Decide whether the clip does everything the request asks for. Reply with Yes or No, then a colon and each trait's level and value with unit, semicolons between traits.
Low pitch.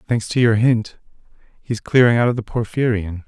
Yes: low, 115 Hz